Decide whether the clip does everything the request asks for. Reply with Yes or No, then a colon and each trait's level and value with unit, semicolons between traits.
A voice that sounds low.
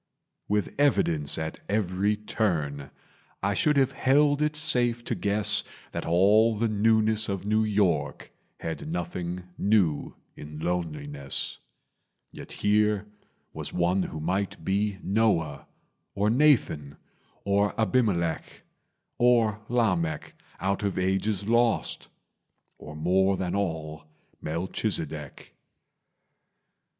Yes: low, 100 Hz